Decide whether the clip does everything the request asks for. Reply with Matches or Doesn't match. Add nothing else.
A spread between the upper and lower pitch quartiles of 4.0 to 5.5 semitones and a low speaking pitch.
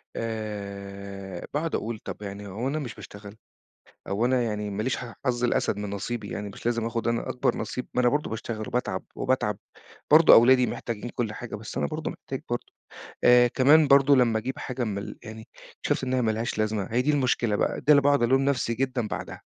Doesn't match